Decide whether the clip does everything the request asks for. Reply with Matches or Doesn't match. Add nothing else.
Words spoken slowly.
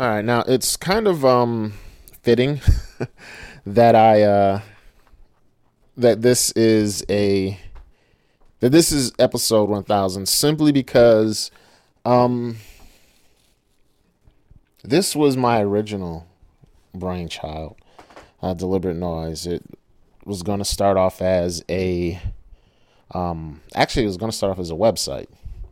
Matches